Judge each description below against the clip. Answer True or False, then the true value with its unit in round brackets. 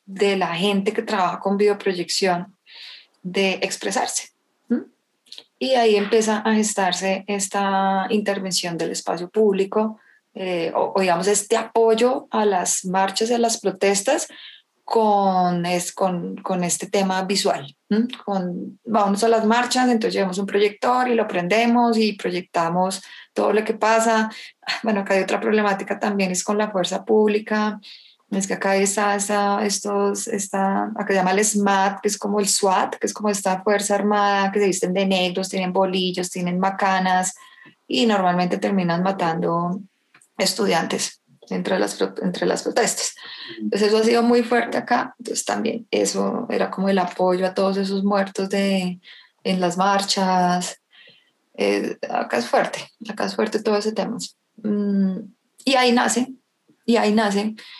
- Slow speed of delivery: False (155 wpm)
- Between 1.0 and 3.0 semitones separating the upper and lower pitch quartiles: True (2.4 semitones)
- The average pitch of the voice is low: False (200 Hz)